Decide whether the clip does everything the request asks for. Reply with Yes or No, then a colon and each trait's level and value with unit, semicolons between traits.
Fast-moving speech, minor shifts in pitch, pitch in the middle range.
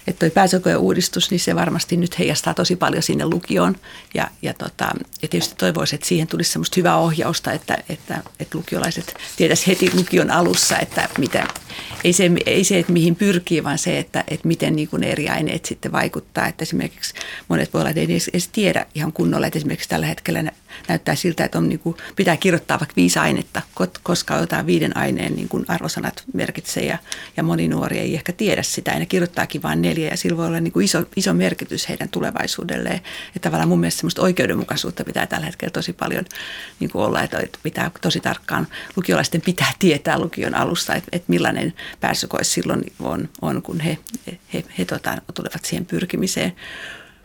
Yes: fast, 190 wpm; narrow, 2.3 semitones; medium, 170 Hz